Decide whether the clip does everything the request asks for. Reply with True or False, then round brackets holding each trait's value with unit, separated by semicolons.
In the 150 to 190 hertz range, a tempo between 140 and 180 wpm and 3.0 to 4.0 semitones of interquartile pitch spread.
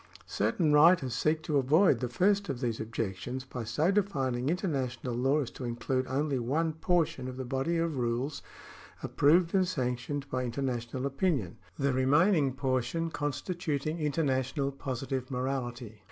False (135 Hz; 145 wpm; 3.7 semitones)